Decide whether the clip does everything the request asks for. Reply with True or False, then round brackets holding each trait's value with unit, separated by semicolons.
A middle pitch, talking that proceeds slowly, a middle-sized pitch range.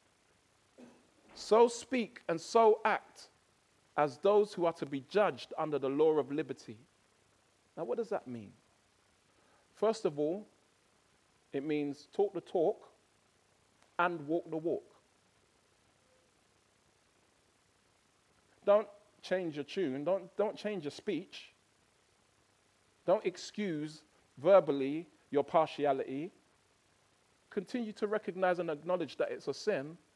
False (175 Hz; 115 wpm; 5.7 semitones)